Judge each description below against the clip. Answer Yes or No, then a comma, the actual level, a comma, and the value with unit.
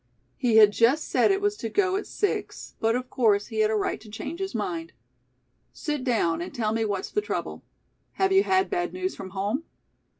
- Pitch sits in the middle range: No, high, 235 Hz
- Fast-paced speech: Yes, fast, 210 wpm